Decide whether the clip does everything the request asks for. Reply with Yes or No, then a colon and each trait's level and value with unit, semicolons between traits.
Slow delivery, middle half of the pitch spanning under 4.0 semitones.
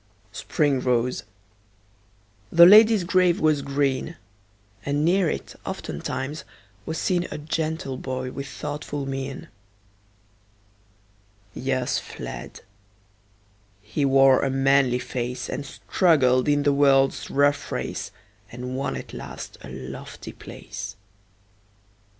Yes: slow, 110 wpm; average, 3.0 semitones